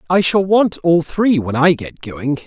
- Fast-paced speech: Yes, fast, 220 wpm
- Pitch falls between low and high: Yes, medium, 165 Hz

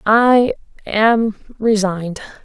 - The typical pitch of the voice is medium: No, high, 215 Hz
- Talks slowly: Yes, slow, 75 wpm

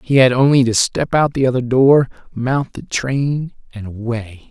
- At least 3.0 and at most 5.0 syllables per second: Yes, 4.2 syllables/s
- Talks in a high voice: No, low, 125 Hz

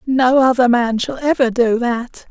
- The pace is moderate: Yes, average, 180 wpm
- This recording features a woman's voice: No, male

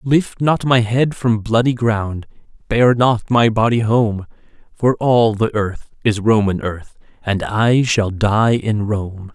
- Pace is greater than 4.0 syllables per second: No, 3.5 syllables/s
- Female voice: No, male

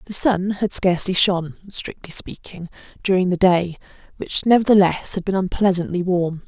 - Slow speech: Yes, slow, 130 wpm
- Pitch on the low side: No, medium, 185 Hz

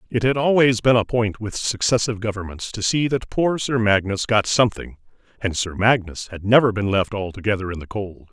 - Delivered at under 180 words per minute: No, average, 200 wpm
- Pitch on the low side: Yes, low, 110 Hz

